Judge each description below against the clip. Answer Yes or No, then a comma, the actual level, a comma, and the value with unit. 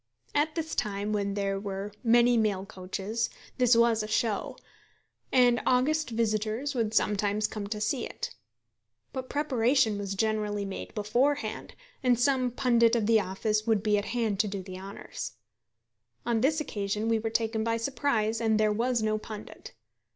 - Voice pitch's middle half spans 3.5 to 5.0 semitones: No, average, 2.7 semitones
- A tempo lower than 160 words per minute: No, average, 165 wpm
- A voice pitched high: Yes, high, 220 Hz